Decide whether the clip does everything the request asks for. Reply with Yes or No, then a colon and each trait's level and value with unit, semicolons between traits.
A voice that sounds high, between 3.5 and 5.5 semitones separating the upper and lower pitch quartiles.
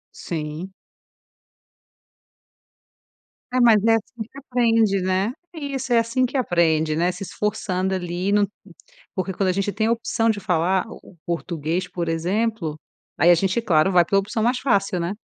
Yes: high, 195 Hz; average, 4.4 semitones